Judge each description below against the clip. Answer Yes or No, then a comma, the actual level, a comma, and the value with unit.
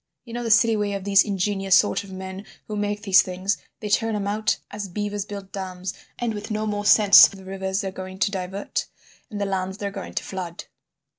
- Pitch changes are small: Yes, narrow, 1.5 semitones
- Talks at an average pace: No, fast, 225 wpm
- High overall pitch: Yes, high, 200 Hz